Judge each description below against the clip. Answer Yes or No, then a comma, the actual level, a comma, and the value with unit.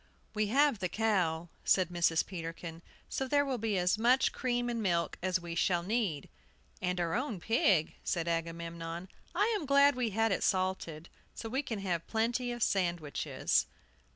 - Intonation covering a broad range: Yes, wide, 5.8 semitones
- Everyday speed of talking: Yes, average, 170 wpm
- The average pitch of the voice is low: No, high, 190 Hz